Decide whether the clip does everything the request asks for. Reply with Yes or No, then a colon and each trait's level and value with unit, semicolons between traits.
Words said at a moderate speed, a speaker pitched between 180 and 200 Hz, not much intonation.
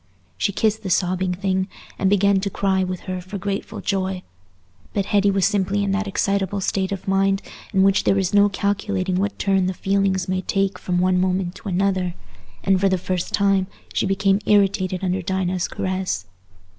Yes: average, 185 wpm; high, 190 Hz; narrow, 1.1 semitones